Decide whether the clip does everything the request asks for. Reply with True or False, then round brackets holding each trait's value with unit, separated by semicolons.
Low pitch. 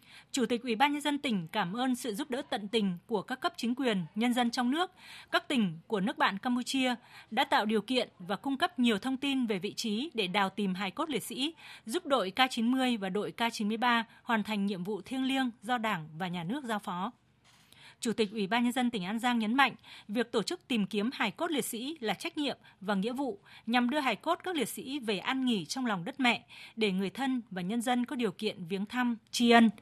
False (235 Hz)